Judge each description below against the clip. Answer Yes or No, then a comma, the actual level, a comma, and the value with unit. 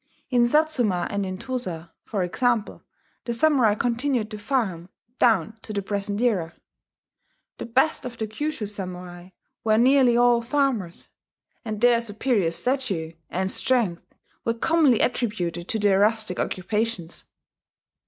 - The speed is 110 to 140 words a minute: Yes, slow, 135 wpm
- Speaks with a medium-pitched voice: No, high, 220 Hz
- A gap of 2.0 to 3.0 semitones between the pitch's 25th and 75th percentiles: No, average, 4.5 semitones